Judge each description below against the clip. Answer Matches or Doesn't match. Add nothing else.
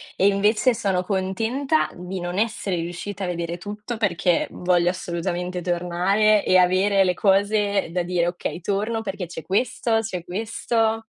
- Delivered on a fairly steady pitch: Doesn't match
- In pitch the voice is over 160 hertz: Matches